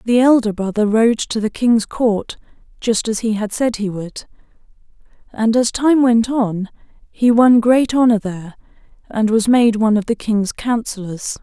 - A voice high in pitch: Yes, high, 225 Hz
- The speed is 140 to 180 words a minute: Yes, average, 175 wpm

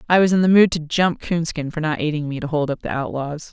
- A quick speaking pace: Yes, fast, 290 wpm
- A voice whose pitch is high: No, medium, 160 Hz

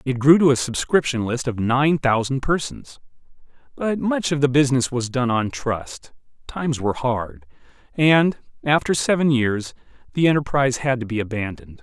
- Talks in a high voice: No, low, 130 Hz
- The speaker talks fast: No, average, 160 wpm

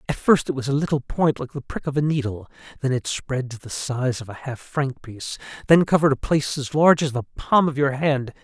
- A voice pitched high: No, low, 135 Hz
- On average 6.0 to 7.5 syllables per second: No, 5.7 syllables/s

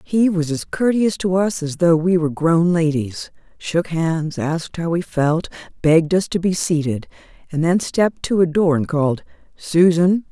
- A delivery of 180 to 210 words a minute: Yes, average, 185 wpm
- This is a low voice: No, medium, 170 Hz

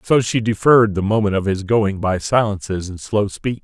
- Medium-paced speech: No, fast, 215 wpm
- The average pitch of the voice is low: Yes, low, 105 Hz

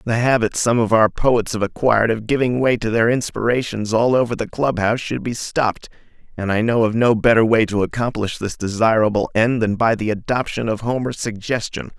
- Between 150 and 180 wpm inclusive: No, fast, 205 wpm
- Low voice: Yes, low, 115 Hz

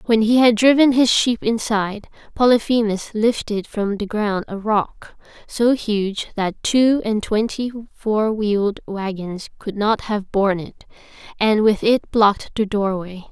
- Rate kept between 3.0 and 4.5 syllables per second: Yes, 4.2 syllables/s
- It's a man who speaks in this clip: No, female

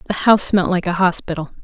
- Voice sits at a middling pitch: Yes, medium, 180 Hz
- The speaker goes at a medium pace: No, fast, 220 wpm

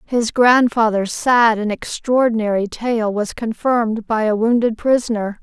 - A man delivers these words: No, female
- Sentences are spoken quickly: No, slow, 135 wpm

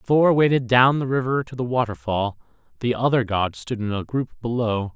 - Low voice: Yes, low, 120 Hz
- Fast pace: No, average, 195 wpm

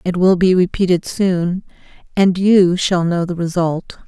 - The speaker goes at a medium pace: Yes, average, 160 wpm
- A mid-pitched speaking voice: Yes, medium, 180 Hz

